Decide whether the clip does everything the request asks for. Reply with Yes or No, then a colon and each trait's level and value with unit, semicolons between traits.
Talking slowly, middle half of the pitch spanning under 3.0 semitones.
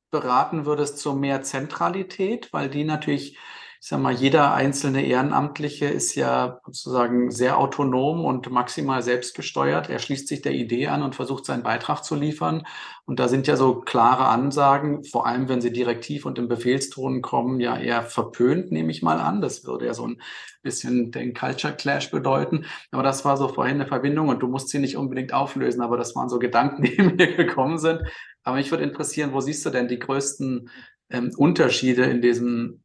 No: average, 190 wpm; narrow, 2.5 semitones